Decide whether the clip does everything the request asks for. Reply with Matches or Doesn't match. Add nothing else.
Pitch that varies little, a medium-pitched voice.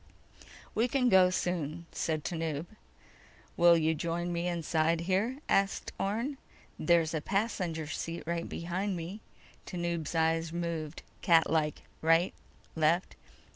Matches